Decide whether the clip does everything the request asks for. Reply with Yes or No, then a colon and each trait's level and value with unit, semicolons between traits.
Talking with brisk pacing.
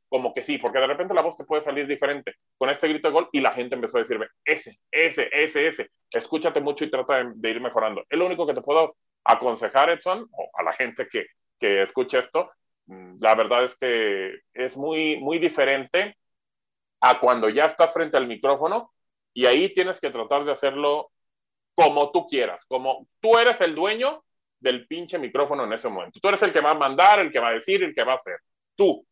Yes: fast, 210 wpm